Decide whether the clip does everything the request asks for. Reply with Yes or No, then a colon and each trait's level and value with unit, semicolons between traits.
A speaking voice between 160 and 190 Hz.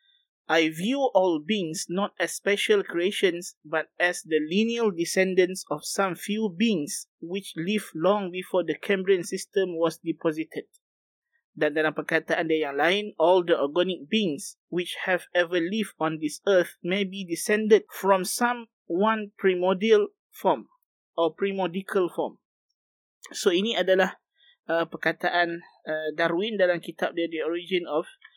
Yes: medium, 185 Hz